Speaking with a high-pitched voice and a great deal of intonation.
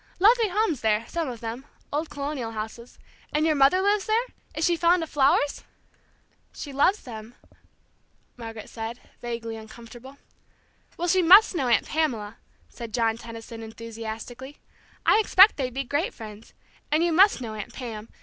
Yes: very high, 255 Hz; wide, 6.4 semitones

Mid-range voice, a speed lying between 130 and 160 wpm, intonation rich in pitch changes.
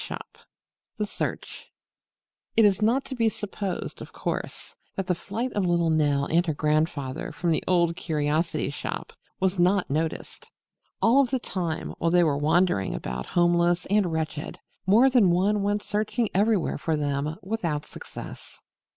No: medium, 175 Hz; average, 155 wpm; average, 4.7 semitones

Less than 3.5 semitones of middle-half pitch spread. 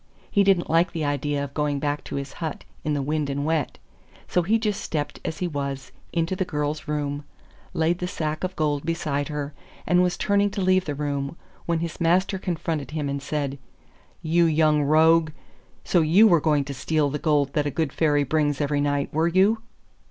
Yes: average, 2.8 semitones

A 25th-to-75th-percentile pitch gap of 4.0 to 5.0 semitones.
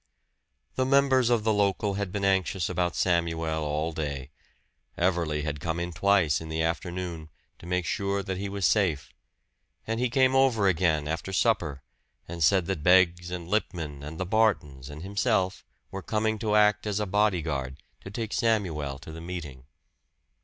Yes: average, 4.3 semitones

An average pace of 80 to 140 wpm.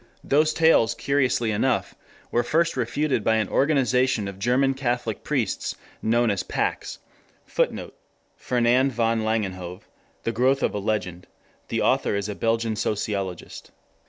Yes: slow, 135 wpm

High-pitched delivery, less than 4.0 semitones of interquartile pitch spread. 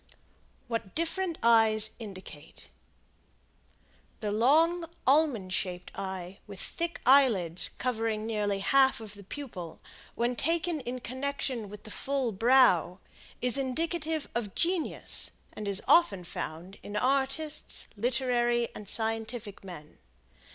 No: high, 230 Hz; average, 5.3 semitones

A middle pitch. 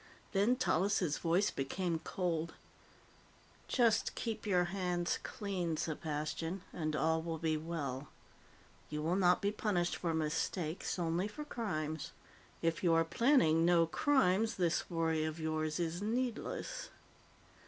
Yes: medium, 170 Hz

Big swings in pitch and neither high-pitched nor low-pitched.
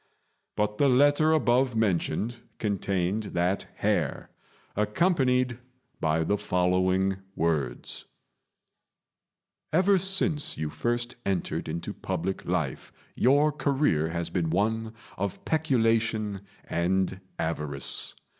No: wide, 6.3 semitones; low, 105 Hz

